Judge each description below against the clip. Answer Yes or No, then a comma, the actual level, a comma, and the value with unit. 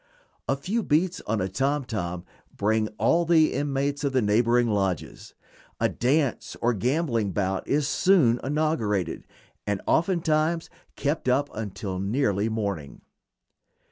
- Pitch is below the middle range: Yes, low, 125 Hz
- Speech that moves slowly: Yes, slow, 130 wpm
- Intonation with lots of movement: Yes, wide, 6.4 semitones